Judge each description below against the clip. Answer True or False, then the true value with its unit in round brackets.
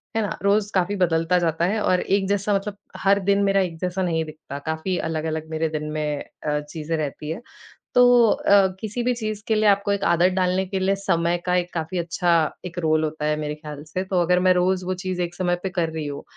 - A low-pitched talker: False (180 Hz)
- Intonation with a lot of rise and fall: False (3.6 semitones)